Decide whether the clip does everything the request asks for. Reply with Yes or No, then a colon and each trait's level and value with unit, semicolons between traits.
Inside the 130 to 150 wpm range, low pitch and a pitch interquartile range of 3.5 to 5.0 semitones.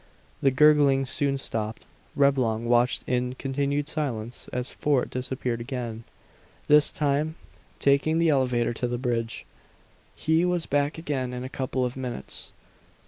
No: average, 140 wpm; low, 130 Hz; average, 2.8 semitones